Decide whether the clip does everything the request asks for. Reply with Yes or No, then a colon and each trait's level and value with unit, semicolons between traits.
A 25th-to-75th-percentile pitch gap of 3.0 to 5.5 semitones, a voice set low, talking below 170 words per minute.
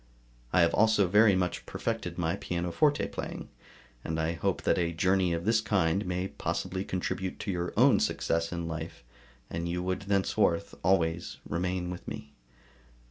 No: narrow, 2.4 semitones; very low, 90 Hz; average, 160 wpm